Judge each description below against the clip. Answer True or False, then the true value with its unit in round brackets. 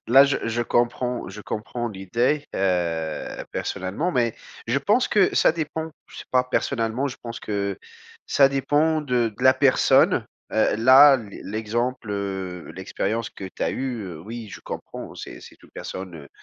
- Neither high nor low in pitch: False (120 Hz)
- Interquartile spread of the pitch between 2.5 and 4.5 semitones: False (5.3 semitones)